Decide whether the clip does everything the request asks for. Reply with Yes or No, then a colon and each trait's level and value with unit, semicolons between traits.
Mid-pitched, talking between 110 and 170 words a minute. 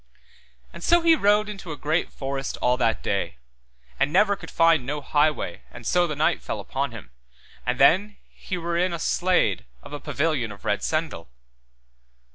No: medium, 155 Hz; average, 185 wpm